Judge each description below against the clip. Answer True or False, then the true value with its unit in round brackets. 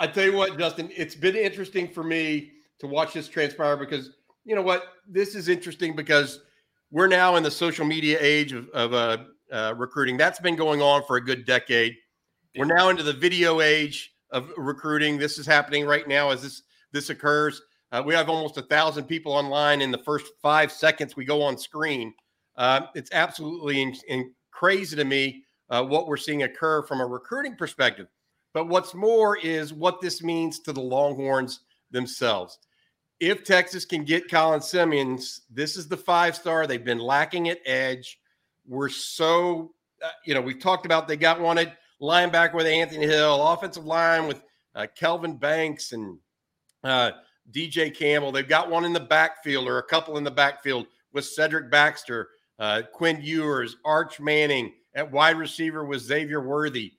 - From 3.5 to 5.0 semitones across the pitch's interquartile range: False (2.8 semitones)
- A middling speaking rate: True (180 wpm)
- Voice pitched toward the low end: False (150 Hz)